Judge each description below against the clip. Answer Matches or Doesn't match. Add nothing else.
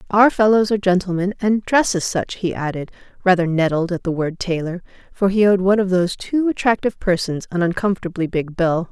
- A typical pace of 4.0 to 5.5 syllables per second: Doesn't match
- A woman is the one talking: Matches